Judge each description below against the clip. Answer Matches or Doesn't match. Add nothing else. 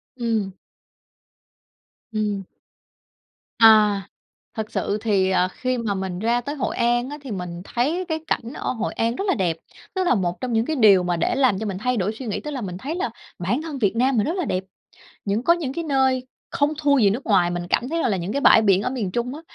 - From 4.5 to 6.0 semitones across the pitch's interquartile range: Matches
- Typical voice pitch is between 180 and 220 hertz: Doesn't match